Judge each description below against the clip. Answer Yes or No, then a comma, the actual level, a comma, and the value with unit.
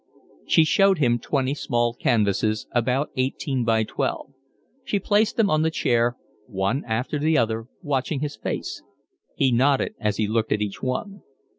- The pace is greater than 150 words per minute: Yes, average, 160 wpm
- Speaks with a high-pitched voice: No, low, 130 Hz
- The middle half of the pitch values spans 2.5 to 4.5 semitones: No, average, 4.9 semitones